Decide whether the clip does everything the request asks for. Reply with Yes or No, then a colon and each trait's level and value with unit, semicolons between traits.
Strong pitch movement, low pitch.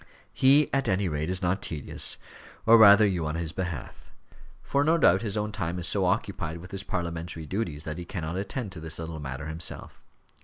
No: average, 4.0 semitones; very low, 90 Hz